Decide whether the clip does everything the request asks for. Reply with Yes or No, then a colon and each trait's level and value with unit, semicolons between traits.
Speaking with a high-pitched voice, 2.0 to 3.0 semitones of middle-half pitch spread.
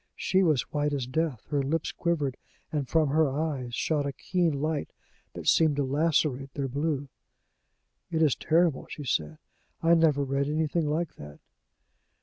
No: medium, 145 Hz; average, 2.7 semitones